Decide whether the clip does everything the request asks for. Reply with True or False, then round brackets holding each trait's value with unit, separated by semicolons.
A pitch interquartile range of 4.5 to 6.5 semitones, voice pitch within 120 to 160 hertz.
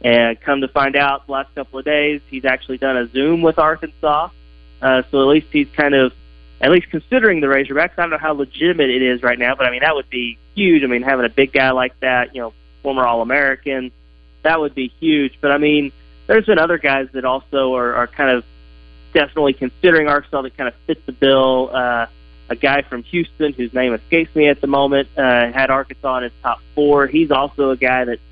False (2.9 semitones; 135 Hz)